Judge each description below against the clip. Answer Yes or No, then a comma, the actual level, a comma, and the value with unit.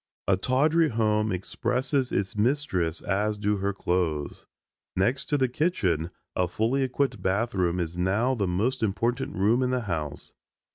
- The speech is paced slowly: No, average, 155 wpm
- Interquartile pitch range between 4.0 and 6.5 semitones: Yes, wide, 5.5 semitones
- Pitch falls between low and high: No, low, 105 Hz